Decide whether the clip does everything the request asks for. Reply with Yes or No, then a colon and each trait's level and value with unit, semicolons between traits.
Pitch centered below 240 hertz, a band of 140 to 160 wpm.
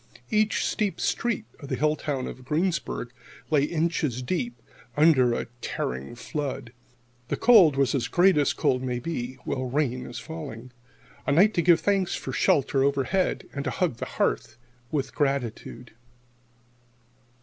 Yes: medium, 140 Hz; average, 150 wpm